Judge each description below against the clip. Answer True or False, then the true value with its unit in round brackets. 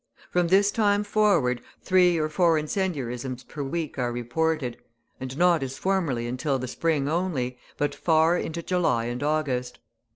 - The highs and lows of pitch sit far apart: True (5.7 semitones)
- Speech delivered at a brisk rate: False (155 wpm)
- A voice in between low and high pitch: True (155 Hz)